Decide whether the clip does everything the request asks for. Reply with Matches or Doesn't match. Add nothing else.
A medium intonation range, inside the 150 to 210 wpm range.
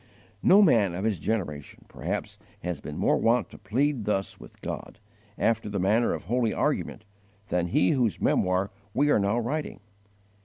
Matches